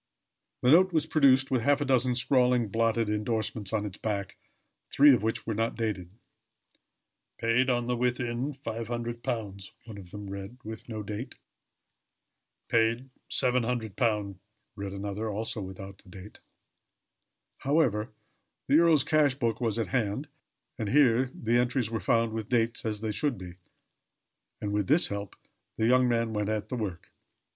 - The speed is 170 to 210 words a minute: No, average, 150 wpm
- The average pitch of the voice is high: No, low, 115 Hz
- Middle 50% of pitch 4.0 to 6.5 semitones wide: No, average, 3.1 semitones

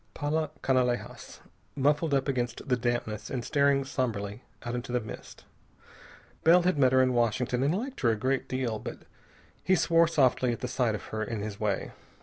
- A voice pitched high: No, low, 130 Hz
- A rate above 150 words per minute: Yes, average, 180 wpm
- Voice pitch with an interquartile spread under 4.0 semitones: Yes, average, 3.2 semitones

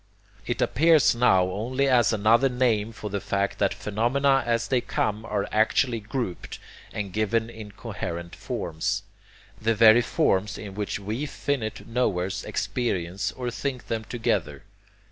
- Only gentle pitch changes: No, average, 3.3 semitones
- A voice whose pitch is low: Yes, low, 110 Hz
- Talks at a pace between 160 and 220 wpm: No, average, 145 wpm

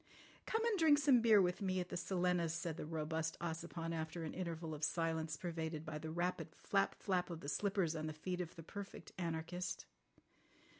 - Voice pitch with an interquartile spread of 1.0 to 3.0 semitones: Yes, narrow, 2.5 semitones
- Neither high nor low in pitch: Yes, medium, 170 Hz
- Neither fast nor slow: Yes, average, 195 wpm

